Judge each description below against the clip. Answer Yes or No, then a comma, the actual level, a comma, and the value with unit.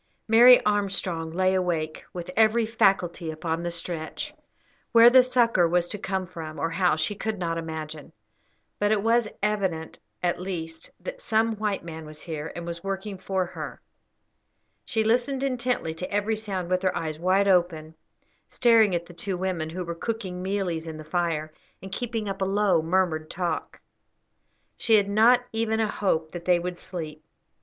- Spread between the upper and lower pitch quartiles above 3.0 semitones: Yes, average, 4.2 semitones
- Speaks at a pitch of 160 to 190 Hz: Yes, medium, 185 Hz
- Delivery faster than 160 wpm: Yes, average, 175 wpm